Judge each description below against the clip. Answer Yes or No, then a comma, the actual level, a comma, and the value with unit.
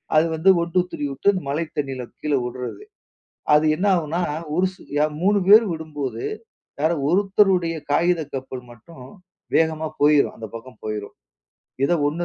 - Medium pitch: Yes, medium, 155 Hz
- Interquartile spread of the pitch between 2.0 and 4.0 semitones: No, average, 4.8 semitones